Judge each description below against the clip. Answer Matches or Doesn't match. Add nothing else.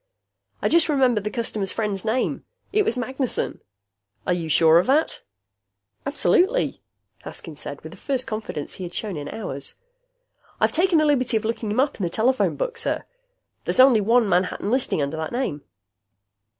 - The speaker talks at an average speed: Matches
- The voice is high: Matches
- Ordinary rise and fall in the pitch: Doesn't match